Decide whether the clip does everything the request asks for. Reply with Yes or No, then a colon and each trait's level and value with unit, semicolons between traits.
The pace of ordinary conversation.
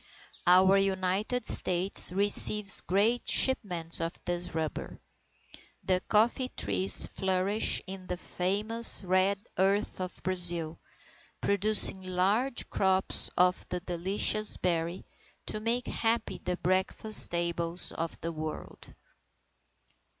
No: slow, 105 wpm